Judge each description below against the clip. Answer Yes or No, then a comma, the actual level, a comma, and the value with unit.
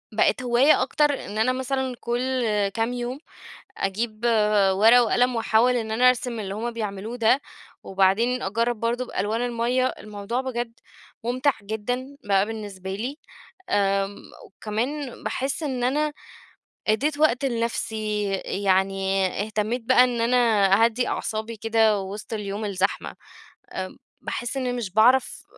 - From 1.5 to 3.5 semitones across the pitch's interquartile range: Yes, average, 3.2 semitones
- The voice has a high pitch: Yes, high, 230 Hz